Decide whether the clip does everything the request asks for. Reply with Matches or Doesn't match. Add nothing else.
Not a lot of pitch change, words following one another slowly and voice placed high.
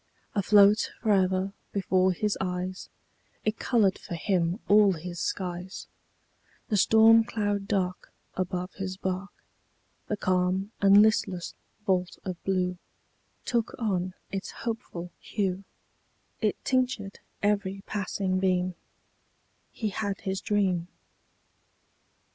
Matches